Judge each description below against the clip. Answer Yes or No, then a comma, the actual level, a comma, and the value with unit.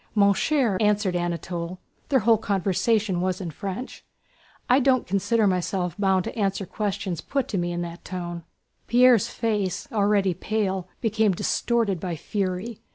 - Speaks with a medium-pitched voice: No, high, 195 Hz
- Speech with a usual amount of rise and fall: Yes, average, 3.3 semitones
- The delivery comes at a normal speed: Yes, average, 150 wpm